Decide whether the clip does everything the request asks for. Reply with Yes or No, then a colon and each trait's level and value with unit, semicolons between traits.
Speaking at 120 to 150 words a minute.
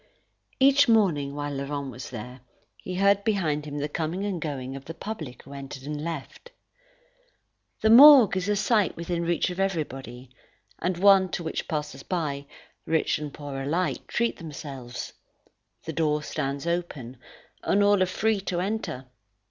No: average, 160 wpm